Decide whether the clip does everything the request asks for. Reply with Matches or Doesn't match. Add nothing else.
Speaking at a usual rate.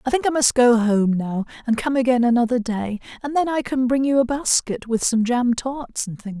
Doesn't match